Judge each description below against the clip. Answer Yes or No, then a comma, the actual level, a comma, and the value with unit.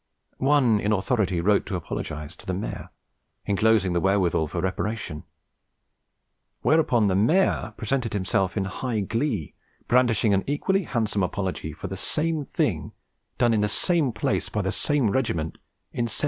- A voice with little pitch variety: No, average, 5.0 semitones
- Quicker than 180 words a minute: No, average, 155 wpm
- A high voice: No, low, 105 Hz